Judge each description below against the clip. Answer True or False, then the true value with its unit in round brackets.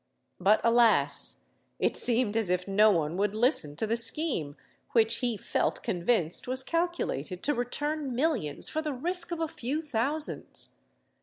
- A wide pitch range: True (7.0 semitones)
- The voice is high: True (235 Hz)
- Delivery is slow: False (155 wpm)